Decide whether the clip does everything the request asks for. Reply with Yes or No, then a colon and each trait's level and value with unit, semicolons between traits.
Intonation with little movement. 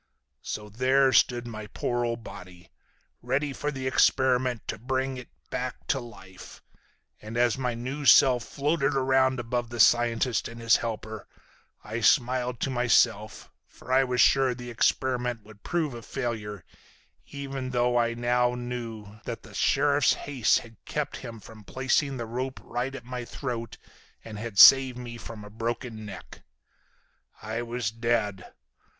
Yes: narrow, 2.3 semitones